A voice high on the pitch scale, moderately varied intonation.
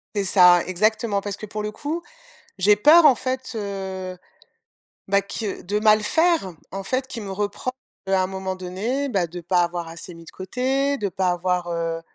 Yes: high, 195 Hz; average, 3.5 semitones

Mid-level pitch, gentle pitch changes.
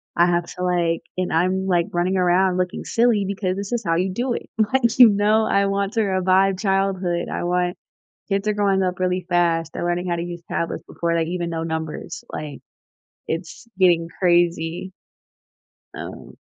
Yes: medium, 180 Hz; narrow, 2.2 semitones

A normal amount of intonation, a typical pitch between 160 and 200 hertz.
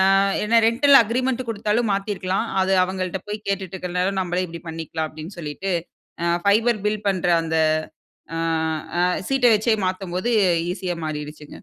Yes: average, 3.5 semitones; high, 190 Hz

